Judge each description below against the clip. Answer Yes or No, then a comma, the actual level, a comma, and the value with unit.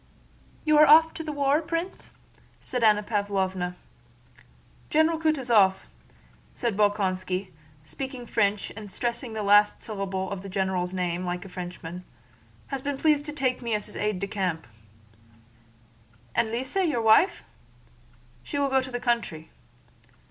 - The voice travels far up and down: Yes, wide, 6.3 semitones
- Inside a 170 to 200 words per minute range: No, average, 145 wpm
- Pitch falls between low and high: No, high, 215 Hz